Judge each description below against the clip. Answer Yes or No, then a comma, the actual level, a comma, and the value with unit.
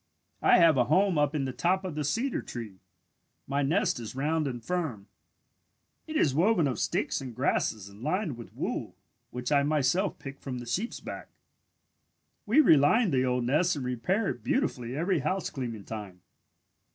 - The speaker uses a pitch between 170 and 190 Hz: No, medium, 145 Hz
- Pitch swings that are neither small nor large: No, wide, 6.3 semitones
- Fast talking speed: No, average, 175 wpm